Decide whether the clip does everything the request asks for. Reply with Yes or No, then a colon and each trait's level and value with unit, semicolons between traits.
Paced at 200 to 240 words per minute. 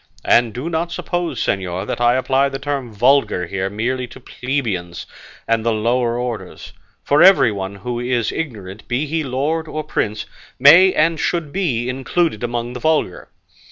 No: average, 160 wpm